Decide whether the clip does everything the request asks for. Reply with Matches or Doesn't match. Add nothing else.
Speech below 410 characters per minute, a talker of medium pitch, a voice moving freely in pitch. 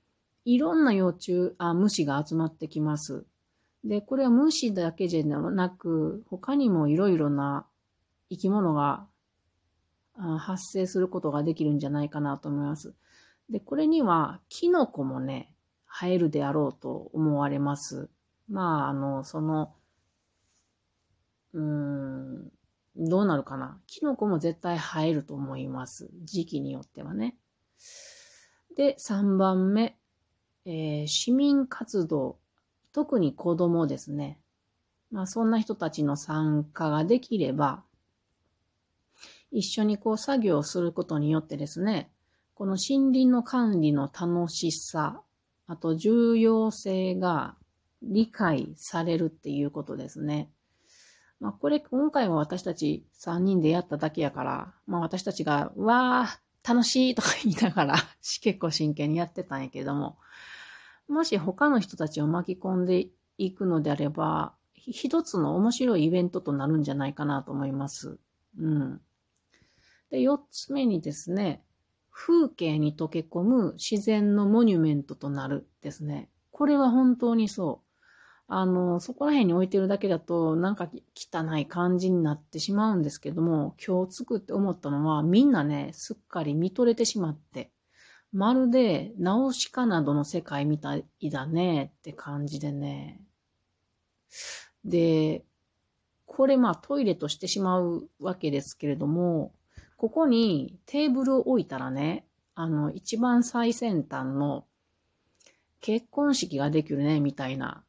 Matches